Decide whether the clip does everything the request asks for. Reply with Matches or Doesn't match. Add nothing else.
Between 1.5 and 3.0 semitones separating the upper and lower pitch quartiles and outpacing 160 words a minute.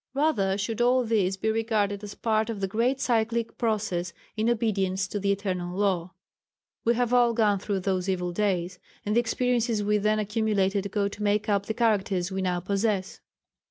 Matches